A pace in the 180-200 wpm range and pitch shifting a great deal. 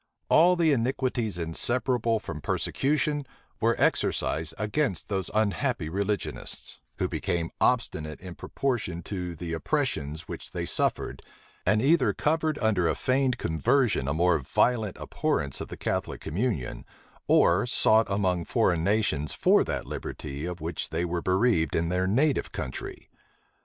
No: average, 140 wpm; wide, 7.0 semitones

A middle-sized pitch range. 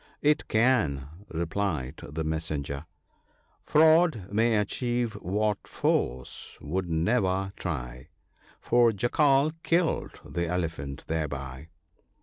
No: wide, 7.8 semitones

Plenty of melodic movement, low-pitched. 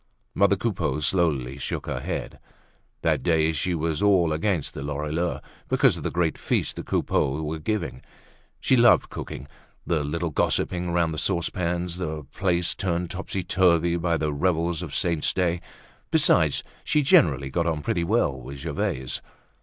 No: average, 2.8 semitones; very low, 85 Hz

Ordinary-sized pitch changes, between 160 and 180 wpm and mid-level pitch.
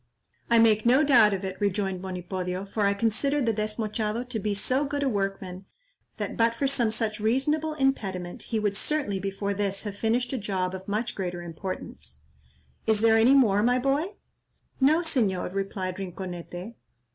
No: average, 4.2 semitones; average, 170 wpm; high, 210 Hz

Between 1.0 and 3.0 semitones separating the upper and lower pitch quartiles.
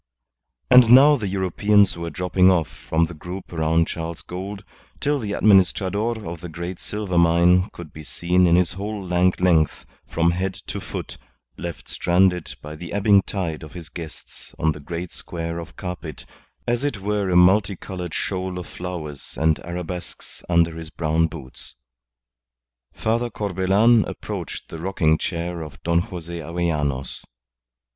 Yes: average, 2.7 semitones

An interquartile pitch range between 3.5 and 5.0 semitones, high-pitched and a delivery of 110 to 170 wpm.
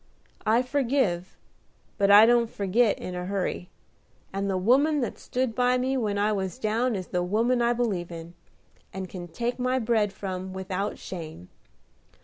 Yes: average, 4.6 semitones; high, 210 Hz; average, 165 wpm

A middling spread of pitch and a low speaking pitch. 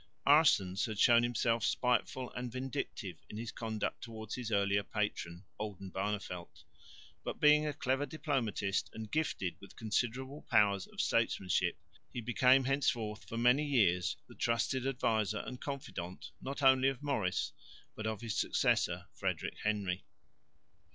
Yes: average, 4.3 semitones; low, 115 Hz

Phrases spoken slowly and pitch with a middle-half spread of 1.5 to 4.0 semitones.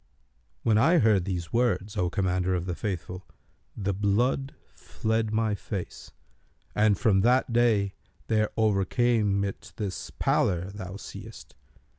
Yes: slow, 130 wpm; average, 2.9 semitones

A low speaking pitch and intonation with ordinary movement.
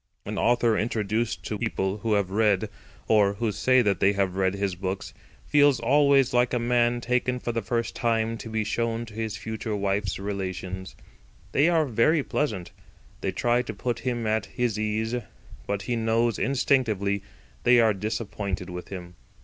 Yes: low, 110 Hz; average, 3.1 semitones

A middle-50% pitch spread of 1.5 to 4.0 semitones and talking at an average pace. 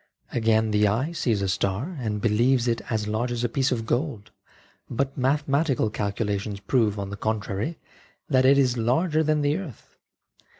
No: average, 4.5 semitones; average, 175 wpm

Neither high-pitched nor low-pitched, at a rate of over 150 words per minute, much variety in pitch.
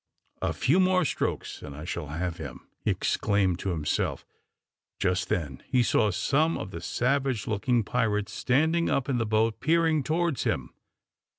No: low, 115 Hz; average, 165 wpm; wide, 7.6 semitones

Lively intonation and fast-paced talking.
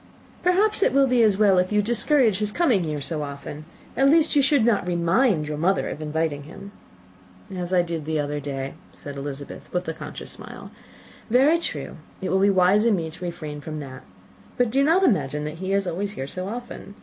Yes: wide, 7.3 semitones; fast, 215 wpm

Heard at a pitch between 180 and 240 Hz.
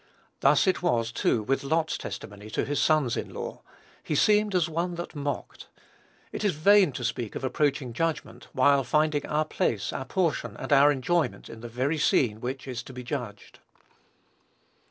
No: medium, 140 Hz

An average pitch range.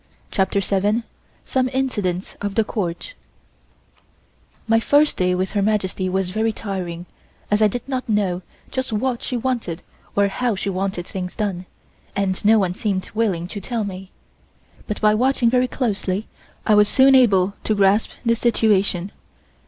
Yes: average, 3.6 semitones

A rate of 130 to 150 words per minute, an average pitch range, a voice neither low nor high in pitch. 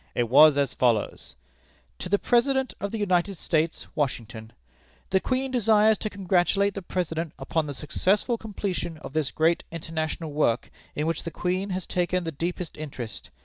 No: average, 165 wpm; average, 4.7 semitones; medium, 170 Hz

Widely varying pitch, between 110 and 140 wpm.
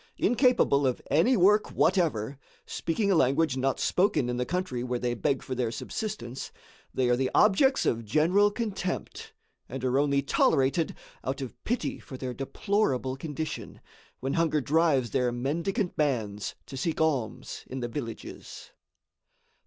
No: wide, 6.0 semitones; average, 150 wpm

